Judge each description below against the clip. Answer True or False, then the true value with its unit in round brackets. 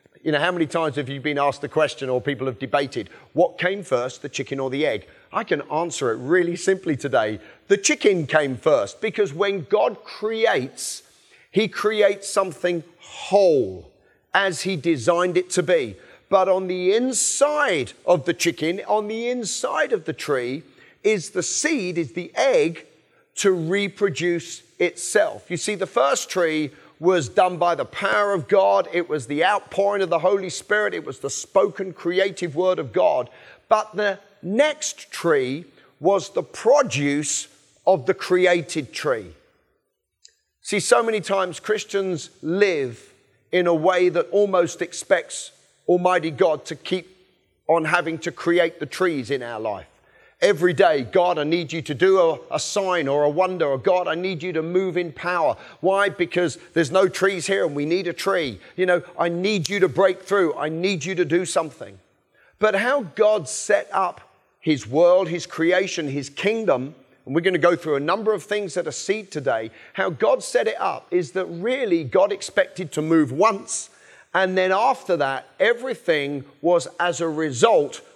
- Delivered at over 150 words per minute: True (175 wpm)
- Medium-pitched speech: True (180 Hz)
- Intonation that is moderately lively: True (3.4 semitones)